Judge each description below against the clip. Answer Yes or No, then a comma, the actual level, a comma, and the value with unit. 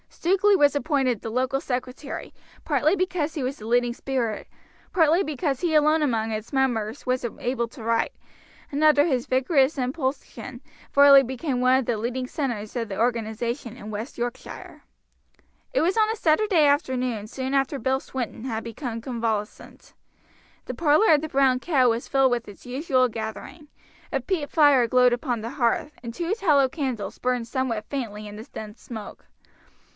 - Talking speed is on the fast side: No, average, 170 wpm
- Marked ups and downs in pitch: No, average, 3.9 semitones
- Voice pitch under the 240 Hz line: No, very high, 260 Hz